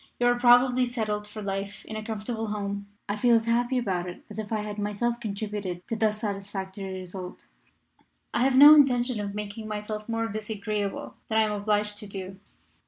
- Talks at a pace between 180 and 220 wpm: Yes, average, 190 wpm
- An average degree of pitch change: No, narrow, 2.2 semitones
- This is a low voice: No, high, 210 Hz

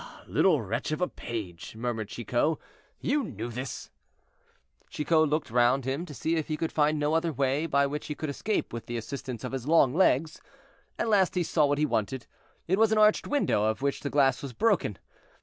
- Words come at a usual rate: No, fast, 210 wpm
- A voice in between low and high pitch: Yes, medium, 145 Hz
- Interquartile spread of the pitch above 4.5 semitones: Yes, average, 4.9 semitones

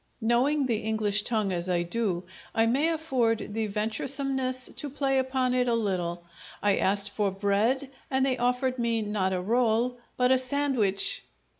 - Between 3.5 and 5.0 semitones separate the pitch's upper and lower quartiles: Yes, average, 4.0 semitones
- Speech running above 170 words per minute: No, average, 165 wpm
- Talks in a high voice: Yes, high, 230 Hz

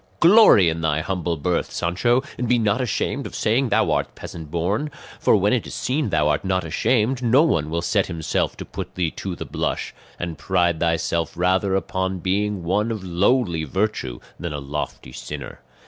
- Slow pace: No, average, 190 wpm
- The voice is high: No, very low, 95 Hz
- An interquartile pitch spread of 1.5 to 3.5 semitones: No, average, 4.7 semitones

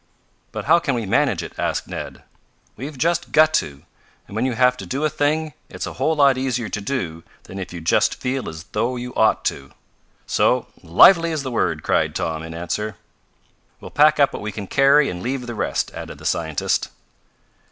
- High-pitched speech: No, low, 125 Hz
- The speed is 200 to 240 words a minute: Yes, fast, 205 wpm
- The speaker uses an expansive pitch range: Yes, wide, 7.8 semitones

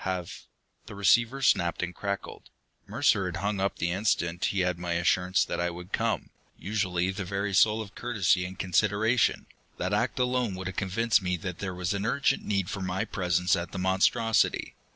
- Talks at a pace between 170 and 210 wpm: Yes, average, 195 wpm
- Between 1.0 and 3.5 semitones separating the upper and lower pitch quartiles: Yes, narrow, 2.5 semitones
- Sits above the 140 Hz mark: No, very low, 95 Hz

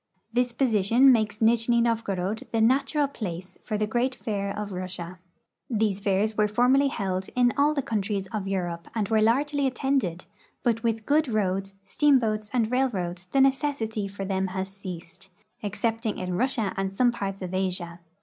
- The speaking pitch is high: Yes, high, 215 Hz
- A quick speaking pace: No, average, 170 wpm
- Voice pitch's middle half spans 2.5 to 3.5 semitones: No, average, 4.3 semitones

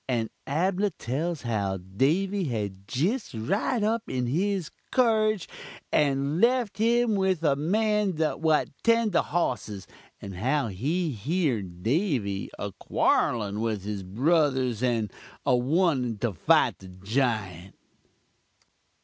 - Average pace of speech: No, slow, 125 wpm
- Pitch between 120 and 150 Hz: Yes, medium, 140 Hz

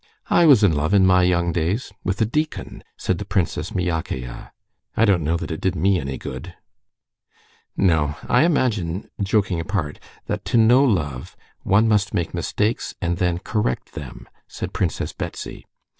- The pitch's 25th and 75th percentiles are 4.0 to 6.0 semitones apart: Yes, average, 4.3 semitones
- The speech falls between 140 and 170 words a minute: Yes, average, 165 wpm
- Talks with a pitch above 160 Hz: No, very low, 95 Hz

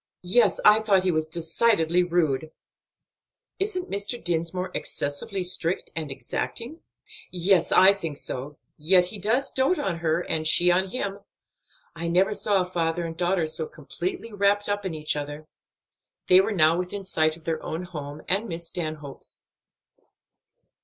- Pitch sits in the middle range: Yes, medium, 180 Hz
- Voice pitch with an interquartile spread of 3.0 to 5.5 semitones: Yes, average, 3.9 semitones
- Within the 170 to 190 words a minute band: No, average, 155 wpm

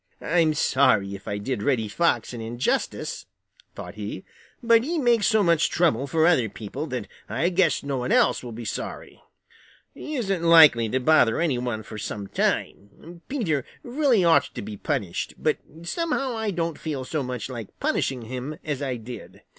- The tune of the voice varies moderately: No, wide, 6.8 semitones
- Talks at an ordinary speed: Yes, average, 180 wpm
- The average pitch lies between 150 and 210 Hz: No, medium, 140 Hz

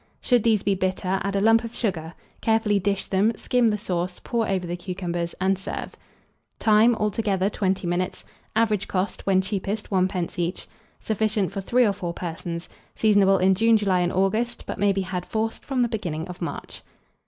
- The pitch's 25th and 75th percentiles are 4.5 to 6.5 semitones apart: No, average, 2.9 semitones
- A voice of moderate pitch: No, high, 195 Hz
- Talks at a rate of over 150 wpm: Yes, average, 185 wpm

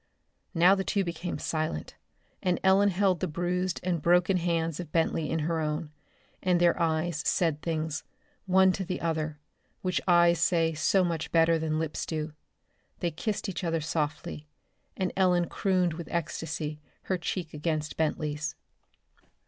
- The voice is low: No, medium, 170 Hz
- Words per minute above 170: No, average, 155 wpm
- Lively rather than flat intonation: No, narrow, 2.4 semitones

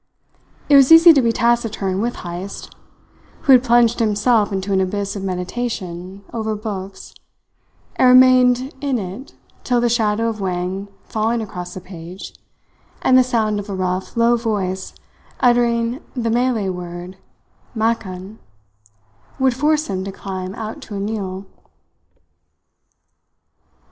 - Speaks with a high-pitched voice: Yes, high, 215 Hz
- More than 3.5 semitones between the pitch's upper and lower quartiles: Yes, average, 4.1 semitones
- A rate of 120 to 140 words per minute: Yes, slow, 135 wpm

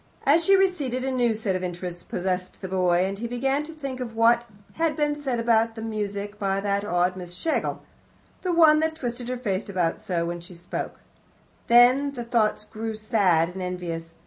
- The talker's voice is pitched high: Yes, high, 220 Hz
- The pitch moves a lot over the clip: Yes, wide, 5.7 semitones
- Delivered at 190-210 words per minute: Yes, average, 195 wpm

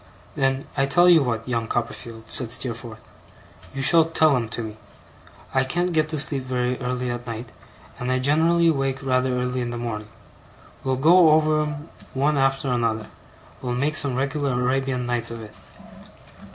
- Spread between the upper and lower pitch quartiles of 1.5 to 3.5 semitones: Yes, average, 3.2 semitones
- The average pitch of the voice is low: Yes, low, 130 Hz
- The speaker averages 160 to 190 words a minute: Yes, average, 175 wpm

